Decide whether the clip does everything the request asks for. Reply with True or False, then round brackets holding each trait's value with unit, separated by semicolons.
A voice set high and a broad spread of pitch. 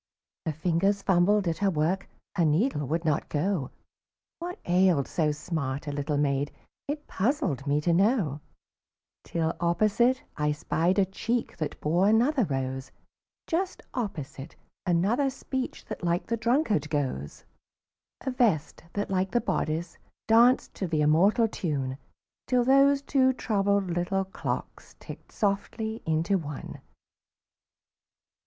False (180 Hz; 6.8 semitones)